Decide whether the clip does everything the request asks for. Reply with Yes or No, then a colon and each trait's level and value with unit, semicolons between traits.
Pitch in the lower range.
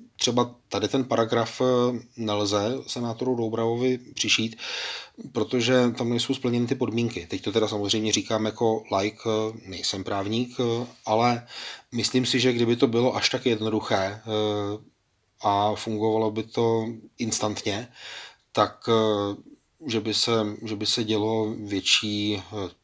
Yes: low, 110 Hz